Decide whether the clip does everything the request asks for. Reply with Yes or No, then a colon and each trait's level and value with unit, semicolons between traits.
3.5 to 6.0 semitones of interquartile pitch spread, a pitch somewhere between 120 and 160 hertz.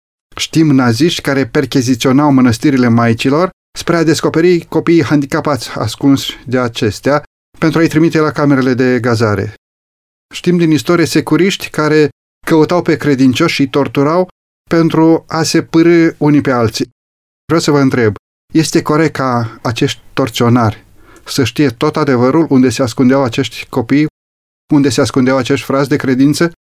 Yes: average, 3.9 semitones; medium, 140 Hz